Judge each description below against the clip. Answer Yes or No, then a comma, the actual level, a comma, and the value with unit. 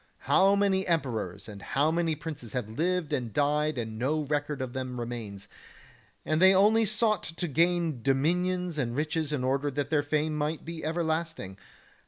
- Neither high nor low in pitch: Yes, medium, 150 Hz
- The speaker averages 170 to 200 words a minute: Yes, average, 175 wpm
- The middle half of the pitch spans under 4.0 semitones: No, average, 4.6 semitones